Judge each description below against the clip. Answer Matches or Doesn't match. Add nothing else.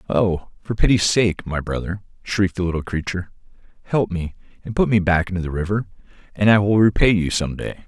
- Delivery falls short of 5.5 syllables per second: Doesn't match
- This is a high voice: Doesn't match